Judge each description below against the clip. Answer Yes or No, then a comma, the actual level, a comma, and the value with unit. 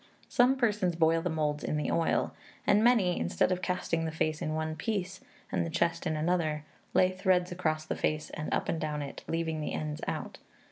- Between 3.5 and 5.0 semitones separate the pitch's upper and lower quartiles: No, average, 2.8 semitones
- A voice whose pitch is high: No, medium, 165 Hz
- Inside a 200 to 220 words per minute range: Yes, fast, 205 wpm